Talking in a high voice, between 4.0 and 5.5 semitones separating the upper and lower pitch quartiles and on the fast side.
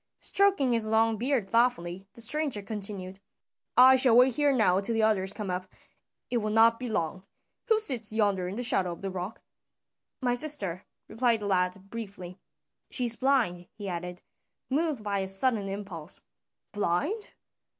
No: high, 215 Hz; average, 4.5 semitones; average, 165 wpm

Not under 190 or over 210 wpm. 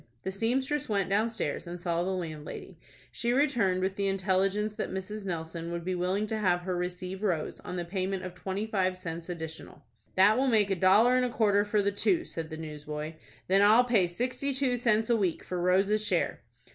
Yes: fast, 205 wpm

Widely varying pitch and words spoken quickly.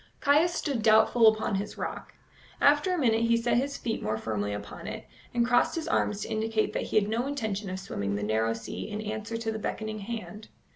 No: average, 3.2 semitones; fast, 215 wpm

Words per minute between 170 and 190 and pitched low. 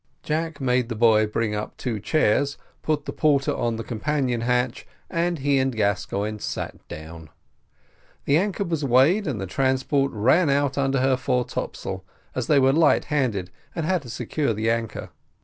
Yes: average, 175 wpm; low, 130 Hz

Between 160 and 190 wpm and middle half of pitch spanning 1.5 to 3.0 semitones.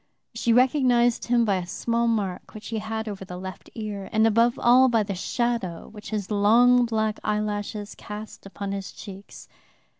Yes: average, 175 wpm; narrow, 2.6 semitones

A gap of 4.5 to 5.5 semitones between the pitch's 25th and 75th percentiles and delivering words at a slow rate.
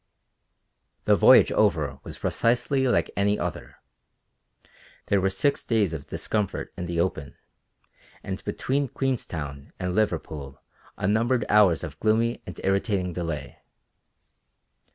Yes: average, 5.2 semitones; slow, 115 wpm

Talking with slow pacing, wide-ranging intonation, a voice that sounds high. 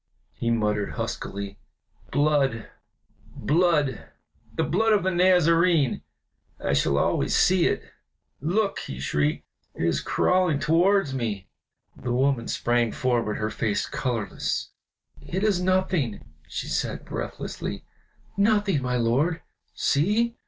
No: slow, 115 wpm; wide, 7.8 semitones; medium, 140 Hz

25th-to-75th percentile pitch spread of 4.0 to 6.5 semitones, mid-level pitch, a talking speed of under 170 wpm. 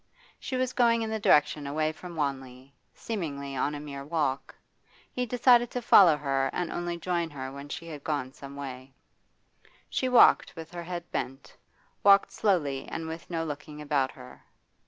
No: average, 4.3 semitones; medium, 155 Hz; average, 175 wpm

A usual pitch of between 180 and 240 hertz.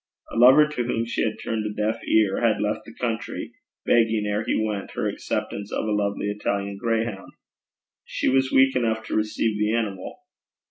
No: low, 110 Hz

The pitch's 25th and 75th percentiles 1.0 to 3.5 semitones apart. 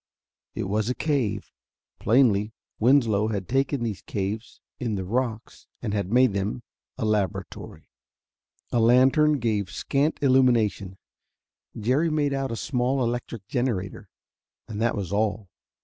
No: average, 4.0 semitones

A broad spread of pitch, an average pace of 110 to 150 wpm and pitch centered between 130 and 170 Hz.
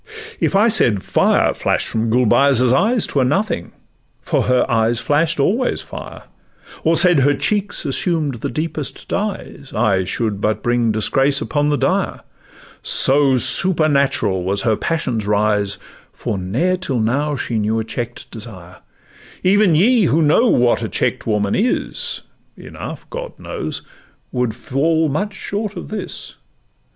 Yes: wide, 7.1 semitones; average, 140 wpm; low, 135 Hz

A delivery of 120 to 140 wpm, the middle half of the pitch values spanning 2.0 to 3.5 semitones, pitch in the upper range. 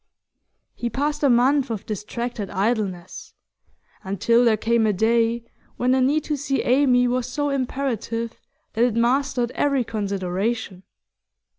Yes: slow, 135 wpm; average, 3.1 semitones; high, 235 Hz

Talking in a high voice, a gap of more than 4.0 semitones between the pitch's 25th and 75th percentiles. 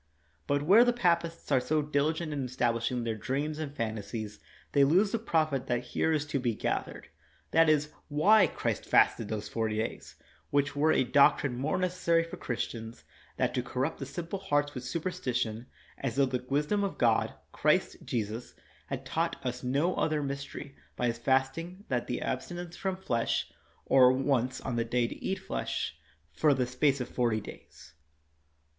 No: low, 135 Hz; average, 4.6 semitones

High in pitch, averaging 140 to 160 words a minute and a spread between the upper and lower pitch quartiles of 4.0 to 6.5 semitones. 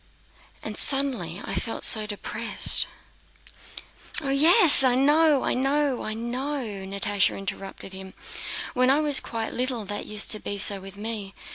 Yes: high, 230 Hz; average, 150 wpm; average, 5.3 semitones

